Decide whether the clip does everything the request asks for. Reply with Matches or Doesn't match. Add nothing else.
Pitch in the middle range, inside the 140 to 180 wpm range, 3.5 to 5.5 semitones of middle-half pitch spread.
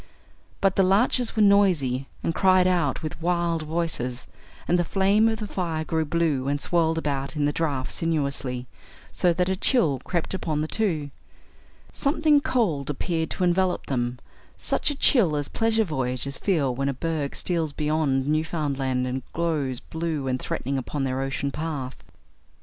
Matches